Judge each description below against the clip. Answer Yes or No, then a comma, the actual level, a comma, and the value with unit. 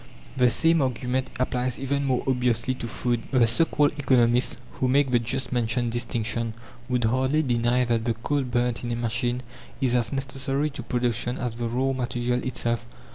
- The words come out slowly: No, average, 180 wpm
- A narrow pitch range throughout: Yes, narrow, 1.8 semitones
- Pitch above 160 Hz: No, low, 125 Hz